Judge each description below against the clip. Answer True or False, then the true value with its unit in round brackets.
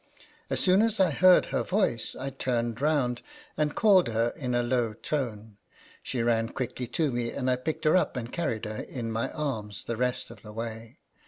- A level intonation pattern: False (4.7 semitones)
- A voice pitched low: True (125 Hz)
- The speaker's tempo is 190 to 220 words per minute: True (200 wpm)